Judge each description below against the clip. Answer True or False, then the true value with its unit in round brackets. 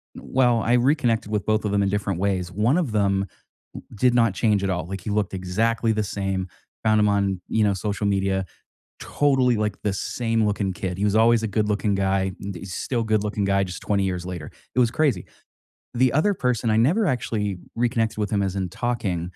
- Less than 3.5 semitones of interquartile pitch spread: True (3.0 semitones)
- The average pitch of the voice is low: True (105 Hz)